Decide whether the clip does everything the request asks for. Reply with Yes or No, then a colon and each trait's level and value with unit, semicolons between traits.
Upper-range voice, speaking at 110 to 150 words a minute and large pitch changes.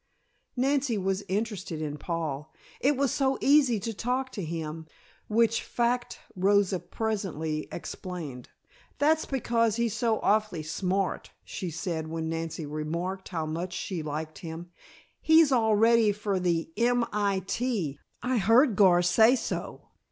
Yes: high, 195 Hz; average, 140 wpm; wide, 6.0 semitones